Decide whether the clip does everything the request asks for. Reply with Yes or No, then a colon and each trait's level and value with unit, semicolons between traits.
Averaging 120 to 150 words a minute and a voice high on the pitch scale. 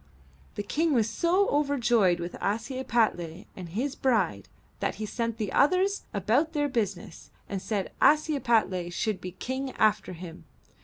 Yes: average, 145 wpm; high, 225 Hz